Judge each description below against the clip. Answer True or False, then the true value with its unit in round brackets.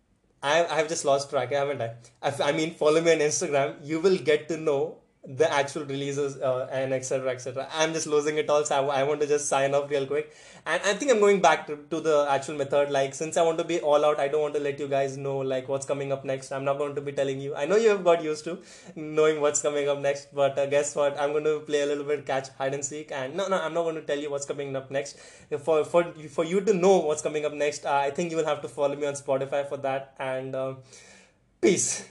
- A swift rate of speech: True (265 wpm)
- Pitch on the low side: False (145 Hz)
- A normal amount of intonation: False (2.1 semitones)